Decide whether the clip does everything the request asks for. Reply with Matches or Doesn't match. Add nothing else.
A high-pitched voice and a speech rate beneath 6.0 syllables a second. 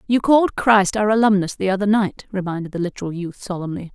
Doesn't match